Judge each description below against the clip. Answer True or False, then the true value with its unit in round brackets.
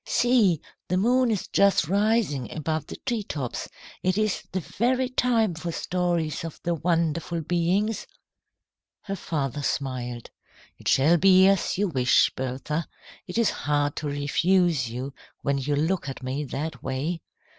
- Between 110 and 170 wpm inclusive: True (150 wpm)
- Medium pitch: True (165 Hz)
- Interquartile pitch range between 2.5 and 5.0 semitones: False (5.4 semitones)